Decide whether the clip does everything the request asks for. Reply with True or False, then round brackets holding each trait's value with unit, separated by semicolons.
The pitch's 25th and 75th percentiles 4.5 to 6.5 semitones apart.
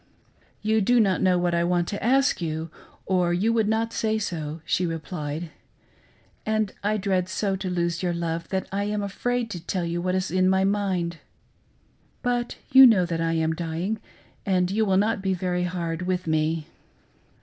False (3.4 semitones)